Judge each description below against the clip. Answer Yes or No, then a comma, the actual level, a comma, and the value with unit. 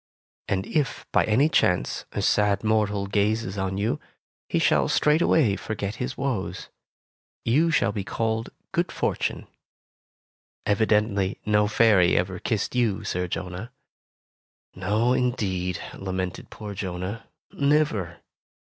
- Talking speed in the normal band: No, slow, 120 wpm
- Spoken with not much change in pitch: No, average, 3.2 semitones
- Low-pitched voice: Yes, low, 105 Hz